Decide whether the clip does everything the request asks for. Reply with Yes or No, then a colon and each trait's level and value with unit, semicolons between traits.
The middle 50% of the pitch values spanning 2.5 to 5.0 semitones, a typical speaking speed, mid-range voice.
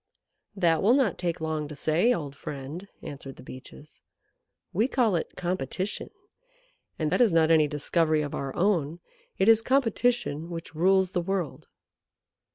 Yes: average, 4.4 semitones; average, 155 wpm; medium, 170 Hz